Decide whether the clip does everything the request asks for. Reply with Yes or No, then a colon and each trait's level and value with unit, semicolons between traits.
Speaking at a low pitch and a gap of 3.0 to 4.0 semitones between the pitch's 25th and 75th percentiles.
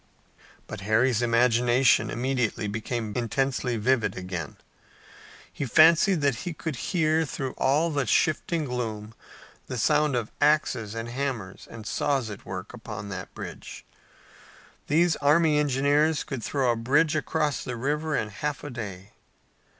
No: low, 130 Hz; average, 4.8 semitones